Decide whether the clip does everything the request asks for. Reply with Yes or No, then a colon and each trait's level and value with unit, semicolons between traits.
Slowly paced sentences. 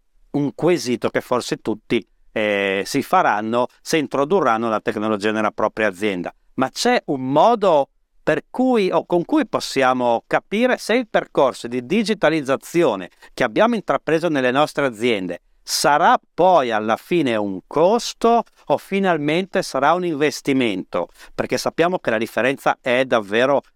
No: average, 140 wpm